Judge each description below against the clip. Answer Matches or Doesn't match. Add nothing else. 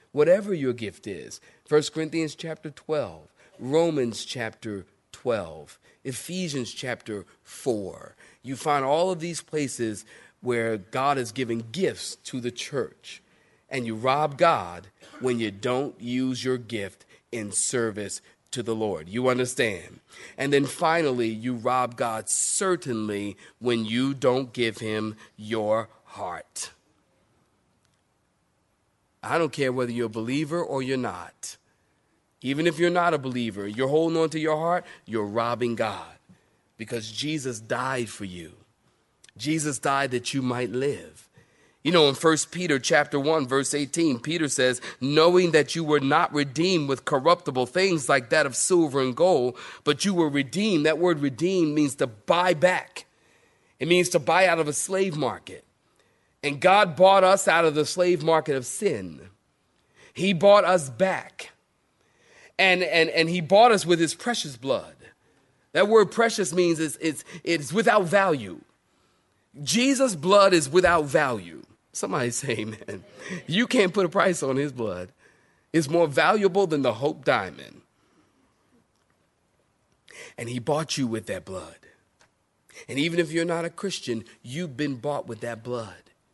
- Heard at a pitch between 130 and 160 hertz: Matches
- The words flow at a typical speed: Matches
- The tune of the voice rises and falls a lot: Matches